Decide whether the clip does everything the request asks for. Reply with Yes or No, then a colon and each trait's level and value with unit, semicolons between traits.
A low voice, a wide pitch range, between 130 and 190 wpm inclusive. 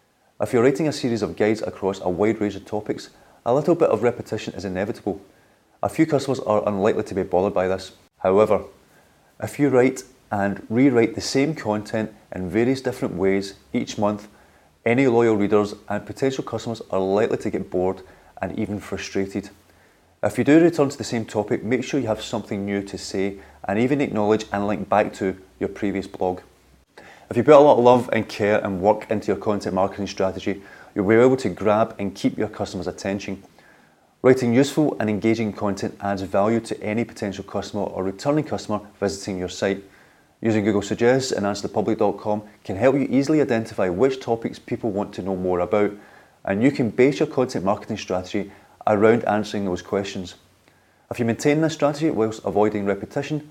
No: low, 105 Hz; average, 3.3 semitones; average, 185 wpm